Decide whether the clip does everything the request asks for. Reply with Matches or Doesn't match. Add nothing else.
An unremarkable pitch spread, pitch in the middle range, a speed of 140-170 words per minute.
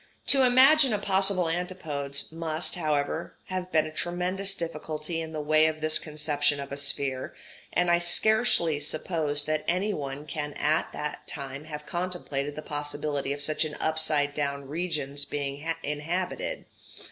Matches